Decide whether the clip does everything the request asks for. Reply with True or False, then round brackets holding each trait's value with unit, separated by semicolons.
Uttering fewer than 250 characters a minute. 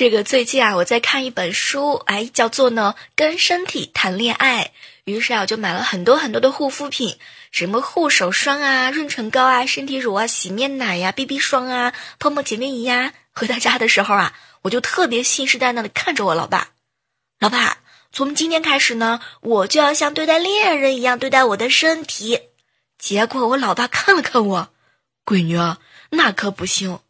False (280 characters per minute)